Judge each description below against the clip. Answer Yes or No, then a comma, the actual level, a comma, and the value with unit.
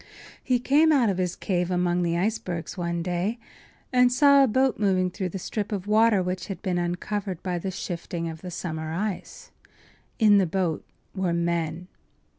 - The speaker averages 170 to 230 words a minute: Yes, average, 180 wpm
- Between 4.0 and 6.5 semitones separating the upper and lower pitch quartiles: No, average, 3.4 semitones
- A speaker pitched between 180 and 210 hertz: Yes, medium, 185 Hz